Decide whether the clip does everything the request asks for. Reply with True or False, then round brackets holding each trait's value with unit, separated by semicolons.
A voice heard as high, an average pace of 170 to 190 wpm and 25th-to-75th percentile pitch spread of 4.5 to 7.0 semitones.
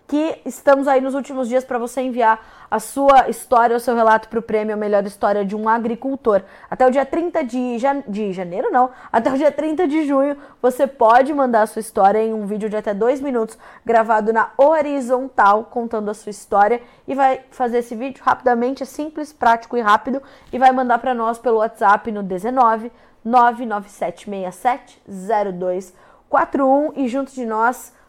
False (240 Hz; 180 wpm; 3.6 semitones)